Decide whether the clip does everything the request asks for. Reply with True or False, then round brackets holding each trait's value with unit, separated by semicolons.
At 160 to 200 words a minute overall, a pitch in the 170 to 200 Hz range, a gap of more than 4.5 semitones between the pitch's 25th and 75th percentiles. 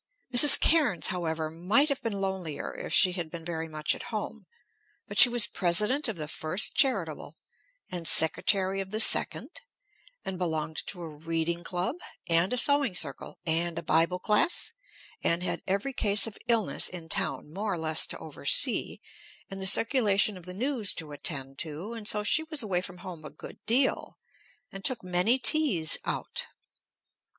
True (175 wpm; 185 Hz; 5.1 semitones)